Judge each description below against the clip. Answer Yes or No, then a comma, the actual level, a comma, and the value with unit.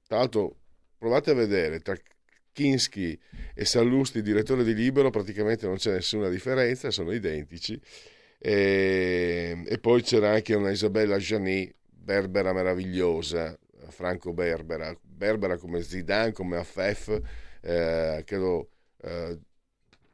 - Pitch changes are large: No, average, 3.9 semitones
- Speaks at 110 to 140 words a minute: Yes, average, 120 wpm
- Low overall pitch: Yes, very low, 95 Hz